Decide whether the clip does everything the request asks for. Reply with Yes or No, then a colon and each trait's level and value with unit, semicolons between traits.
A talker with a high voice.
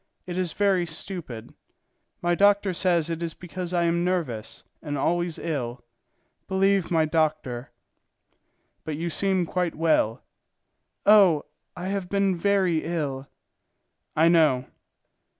No: medium, 170 Hz